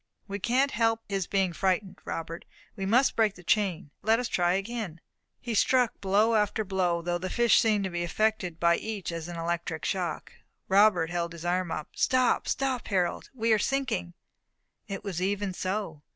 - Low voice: No, high, 195 Hz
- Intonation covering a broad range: No, average, 4.1 semitones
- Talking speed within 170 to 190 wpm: Yes, average, 185 wpm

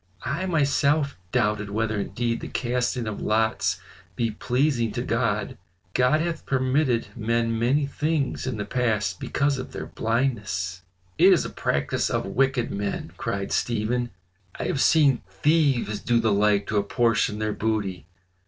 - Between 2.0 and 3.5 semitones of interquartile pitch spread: No, average, 4.1 semitones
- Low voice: Yes, low, 115 Hz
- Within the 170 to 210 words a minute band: No, average, 150 wpm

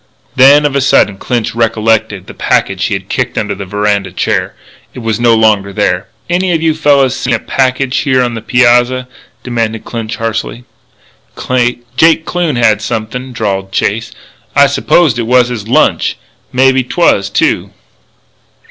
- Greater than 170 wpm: No, average, 165 wpm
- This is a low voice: Yes, low, 120 Hz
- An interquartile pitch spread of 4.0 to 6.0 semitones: No, average, 3.3 semitones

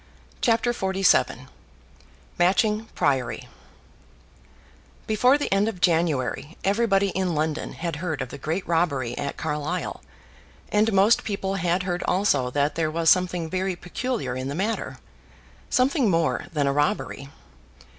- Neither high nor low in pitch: Yes, medium, 175 Hz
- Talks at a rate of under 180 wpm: Yes, slow, 135 wpm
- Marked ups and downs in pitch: No, average, 4.8 semitones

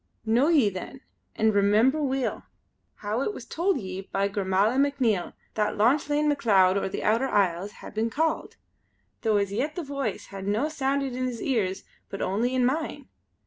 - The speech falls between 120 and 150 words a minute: No, average, 175 wpm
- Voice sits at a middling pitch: No, high, 230 Hz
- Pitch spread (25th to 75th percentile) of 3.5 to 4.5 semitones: No, wide, 5.6 semitones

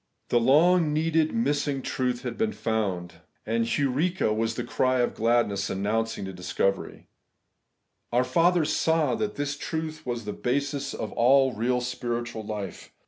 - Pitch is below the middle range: Yes, low, 125 Hz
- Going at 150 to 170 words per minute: Yes, average, 155 wpm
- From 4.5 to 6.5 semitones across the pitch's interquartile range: Yes, average, 5.0 semitones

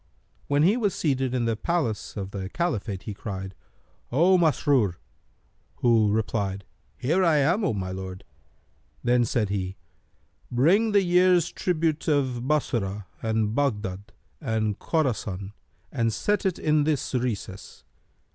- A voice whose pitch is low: Yes, low, 120 Hz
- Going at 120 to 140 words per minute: Yes, slow, 135 wpm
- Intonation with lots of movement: Yes, wide, 7.4 semitones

